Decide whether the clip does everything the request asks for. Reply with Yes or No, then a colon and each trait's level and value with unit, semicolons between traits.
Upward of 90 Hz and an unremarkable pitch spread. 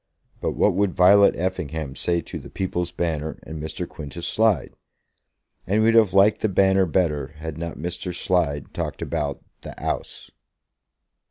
No: very low, 85 Hz; average, 3.4 semitones